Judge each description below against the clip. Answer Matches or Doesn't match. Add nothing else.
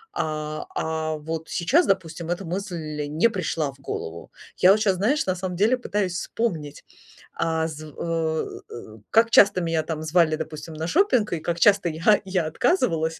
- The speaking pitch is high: Doesn't match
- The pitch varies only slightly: Doesn't match